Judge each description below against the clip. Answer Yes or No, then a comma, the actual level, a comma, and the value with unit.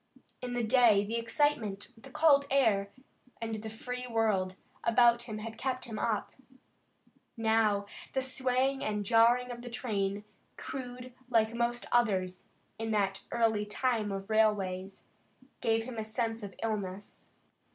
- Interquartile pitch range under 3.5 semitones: Yes, average, 2.9 semitones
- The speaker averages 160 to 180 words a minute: No, average, 140 wpm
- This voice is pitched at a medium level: No, high, 225 Hz